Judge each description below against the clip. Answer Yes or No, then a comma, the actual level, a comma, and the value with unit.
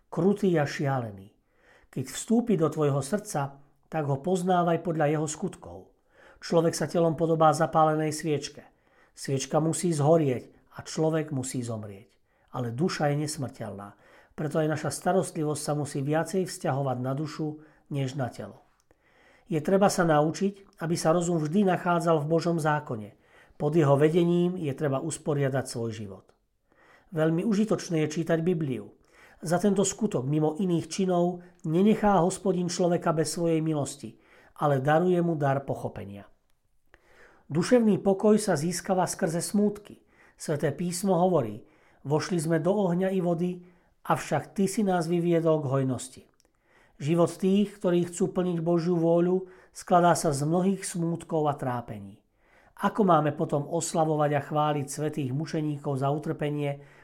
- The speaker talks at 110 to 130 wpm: No, average, 140 wpm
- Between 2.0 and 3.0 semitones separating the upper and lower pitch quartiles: No, average, 3.6 semitones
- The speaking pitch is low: No, medium, 160 Hz